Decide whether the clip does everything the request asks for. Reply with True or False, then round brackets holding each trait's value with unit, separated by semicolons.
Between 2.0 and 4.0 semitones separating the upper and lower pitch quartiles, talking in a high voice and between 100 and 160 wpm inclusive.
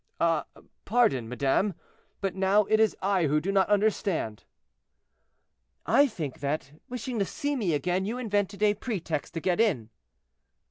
False (5.4 semitones; 195 Hz; 150 wpm)